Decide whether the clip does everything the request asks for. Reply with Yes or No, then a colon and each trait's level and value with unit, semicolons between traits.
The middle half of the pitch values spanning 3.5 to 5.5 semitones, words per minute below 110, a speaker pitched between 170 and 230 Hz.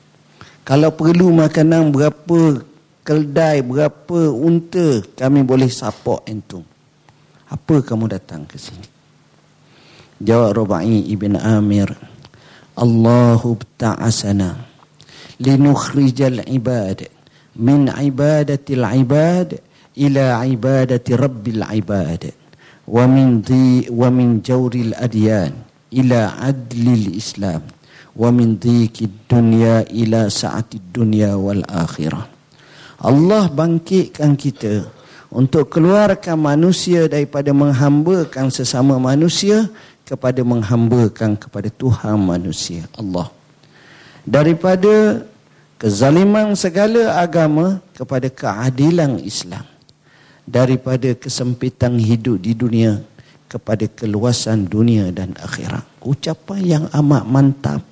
No: average, 4.9 semitones; slow, 90 wpm; low, 130 Hz